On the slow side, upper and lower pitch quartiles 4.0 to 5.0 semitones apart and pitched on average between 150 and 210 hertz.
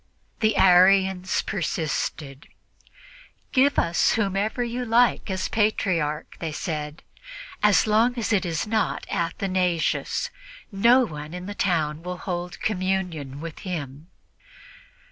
Yes: slow, 115 wpm; average, 4.5 semitones; medium, 185 Hz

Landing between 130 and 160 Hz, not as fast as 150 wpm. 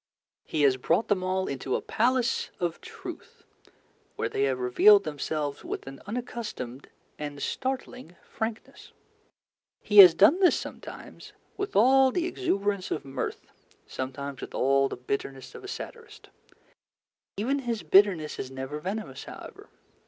No: medium, 185 Hz; average, 140 wpm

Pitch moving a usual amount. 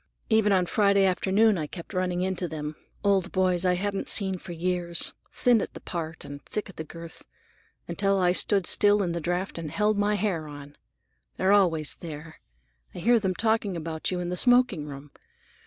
Yes: average, 3.3 semitones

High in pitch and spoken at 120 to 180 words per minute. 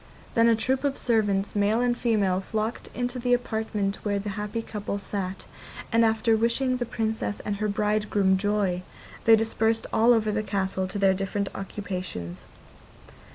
Yes: high, 210 Hz; average, 160 wpm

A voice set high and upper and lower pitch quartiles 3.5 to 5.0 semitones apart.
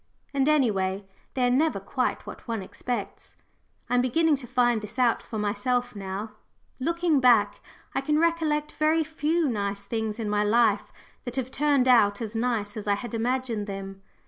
Yes: high, 240 Hz; average, 4.7 semitones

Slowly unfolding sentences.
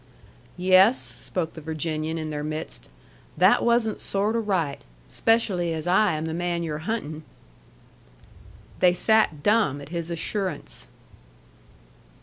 Yes: slow, 130 wpm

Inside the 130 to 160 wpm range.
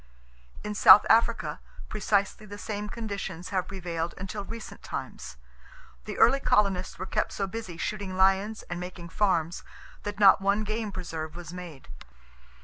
Yes: average, 145 wpm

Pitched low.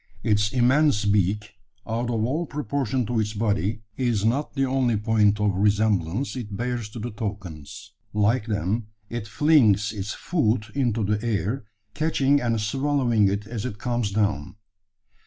Yes: low, 110 Hz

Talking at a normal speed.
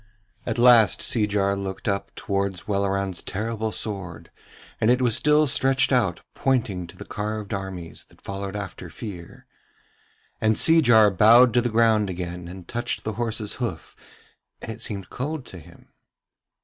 Yes: average, 150 wpm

